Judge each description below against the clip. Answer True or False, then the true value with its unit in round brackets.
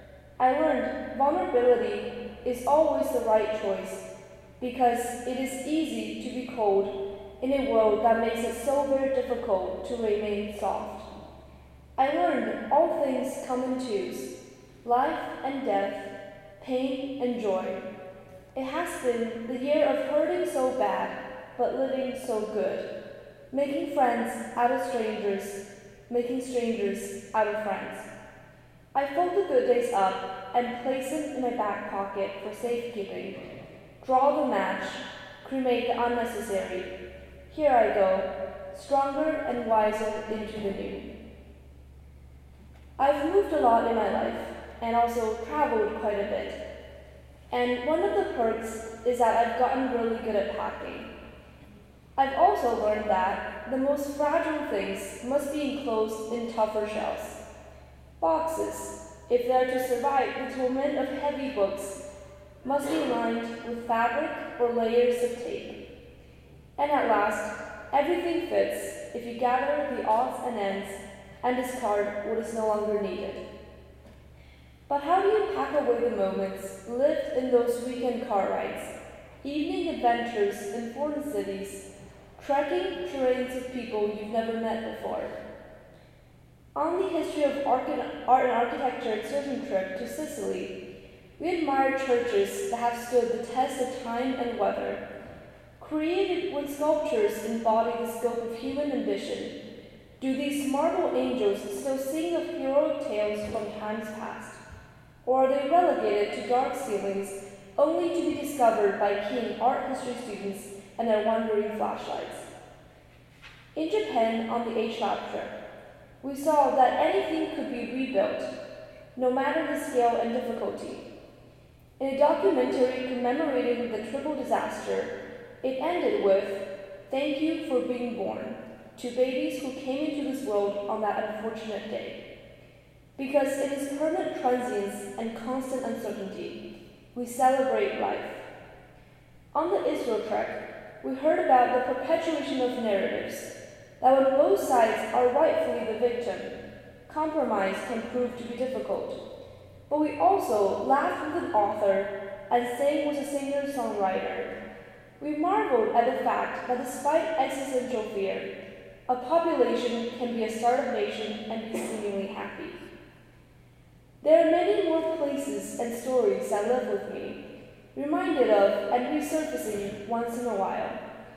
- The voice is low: False (245 Hz)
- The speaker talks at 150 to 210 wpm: False (140 wpm)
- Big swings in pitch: False (4.9 semitones)